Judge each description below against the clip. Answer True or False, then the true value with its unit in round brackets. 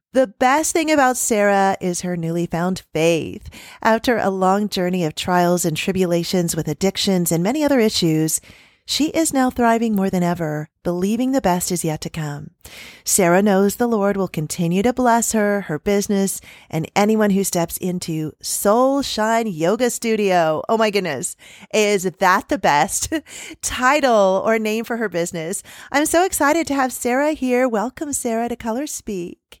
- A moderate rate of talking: True (170 wpm)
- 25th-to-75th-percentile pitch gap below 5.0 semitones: False (5.5 semitones)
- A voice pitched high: True (200 Hz)